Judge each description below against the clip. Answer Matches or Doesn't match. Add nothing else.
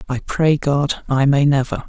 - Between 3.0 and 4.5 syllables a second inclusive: Matches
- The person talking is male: Matches